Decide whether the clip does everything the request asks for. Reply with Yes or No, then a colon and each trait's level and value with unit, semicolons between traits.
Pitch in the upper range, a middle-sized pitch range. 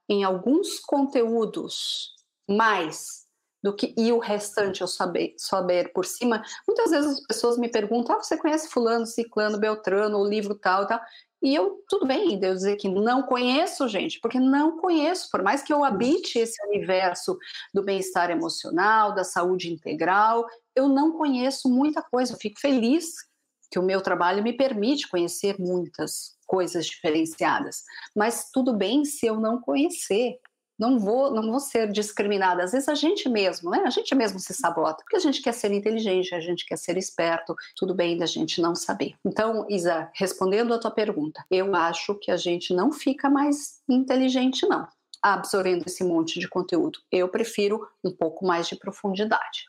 No: high, 220 Hz; wide, 6.3 semitones